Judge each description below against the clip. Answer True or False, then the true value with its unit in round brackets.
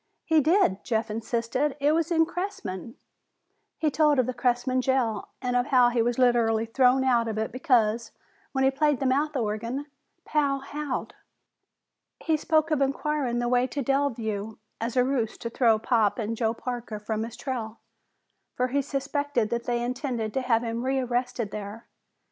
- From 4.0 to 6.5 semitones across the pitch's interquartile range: False (3.3 semitones)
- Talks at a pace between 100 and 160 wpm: False (175 wpm)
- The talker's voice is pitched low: False (250 Hz)